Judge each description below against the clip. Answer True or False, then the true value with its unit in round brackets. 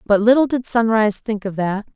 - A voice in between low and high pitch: False (220 Hz)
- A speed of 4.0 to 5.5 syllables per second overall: False (5.8 syllables/s)